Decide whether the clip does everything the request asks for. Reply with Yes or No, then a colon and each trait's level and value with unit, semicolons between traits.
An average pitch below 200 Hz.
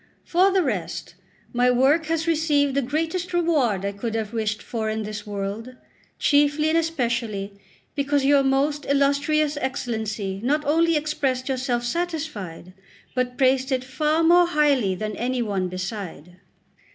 No: very high, 265 Hz